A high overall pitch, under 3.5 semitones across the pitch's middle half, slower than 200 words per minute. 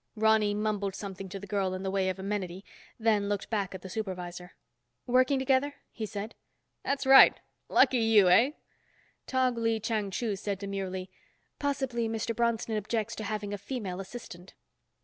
Yes: high, 210 Hz; average, 3.1 semitones; average, 165 wpm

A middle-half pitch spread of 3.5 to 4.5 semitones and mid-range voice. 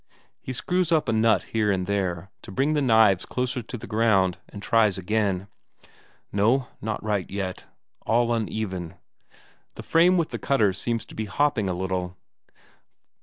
No: average, 4.1 semitones; low, 110 Hz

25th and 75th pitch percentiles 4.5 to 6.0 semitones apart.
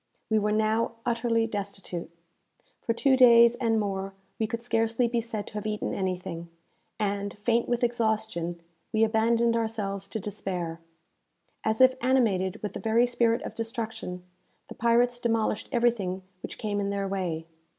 No: average, 2.8 semitones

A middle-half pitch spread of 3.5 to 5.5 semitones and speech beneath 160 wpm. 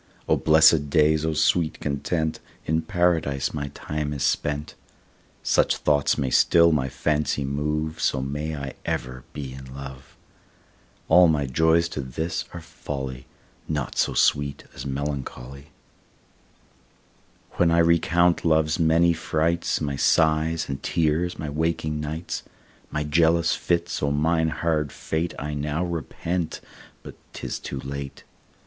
No: narrow, 2.4 semitones; slow, 135 wpm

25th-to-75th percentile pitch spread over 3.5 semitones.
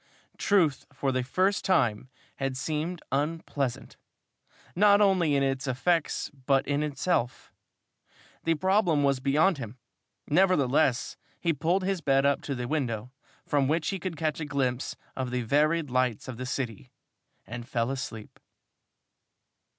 Yes: average, 4.4 semitones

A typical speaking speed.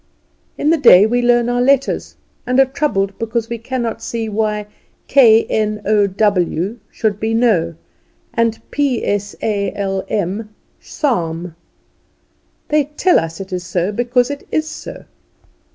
Yes: average, 150 wpm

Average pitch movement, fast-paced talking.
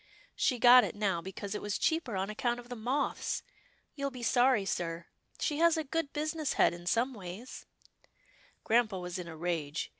No: wide, 6.5 semitones; fast, 210 wpm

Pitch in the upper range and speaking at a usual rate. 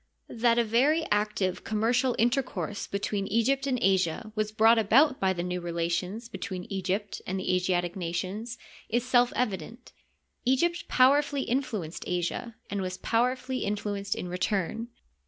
Yes: high, 215 Hz; average, 145 wpm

